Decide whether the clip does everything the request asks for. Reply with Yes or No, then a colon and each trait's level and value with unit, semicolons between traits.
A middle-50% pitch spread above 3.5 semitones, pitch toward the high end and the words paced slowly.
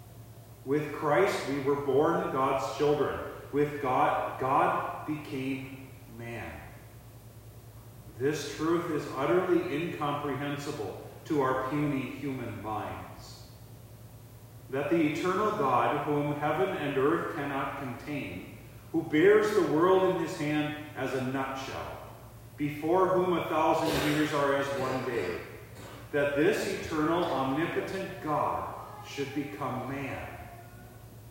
No: average, 4.0 semitones; low, 135 Hz; slow, 115 wpm